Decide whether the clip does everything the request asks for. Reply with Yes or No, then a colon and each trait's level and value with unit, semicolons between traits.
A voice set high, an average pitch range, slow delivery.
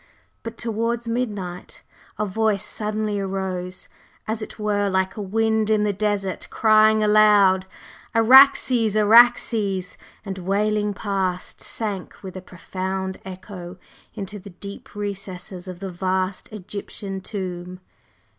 No: high, 200 Hz; narrow, 2.3 semitones; slow, 120 wpm